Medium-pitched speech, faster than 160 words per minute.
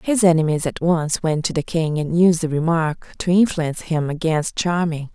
Yes: medium, 165 Hz; average, 200 wpm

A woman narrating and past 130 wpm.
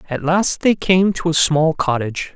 No: male; fast, 205 wpm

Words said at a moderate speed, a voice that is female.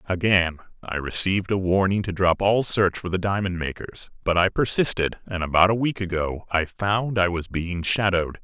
No: average, 190 wpm; male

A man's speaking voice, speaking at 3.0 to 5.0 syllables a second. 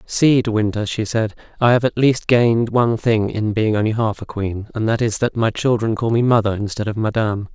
No: male; 5.5 syllables/s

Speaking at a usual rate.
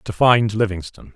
Yes: average, 155 wpm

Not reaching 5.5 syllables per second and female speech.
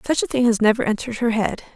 No: 7.0 syllables/s; female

